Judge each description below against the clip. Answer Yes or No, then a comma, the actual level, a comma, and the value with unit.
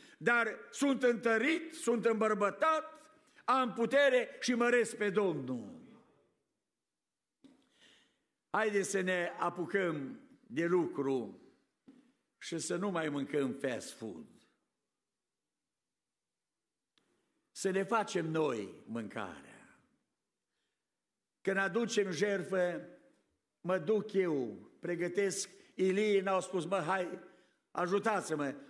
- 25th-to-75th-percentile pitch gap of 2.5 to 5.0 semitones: No, wide, 5.4 semitones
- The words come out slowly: Yes, slow, 90 wpm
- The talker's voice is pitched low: No, high, 200 Hz